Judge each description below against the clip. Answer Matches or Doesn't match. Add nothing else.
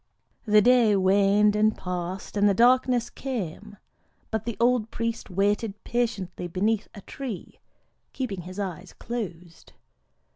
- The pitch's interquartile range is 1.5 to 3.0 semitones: Doesn't match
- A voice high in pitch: Matches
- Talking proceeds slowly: Matches